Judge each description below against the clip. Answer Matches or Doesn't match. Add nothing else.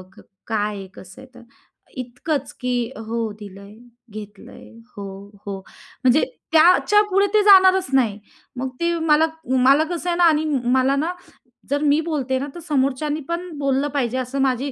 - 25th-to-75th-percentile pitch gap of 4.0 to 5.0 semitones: Matches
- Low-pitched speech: Doesn't match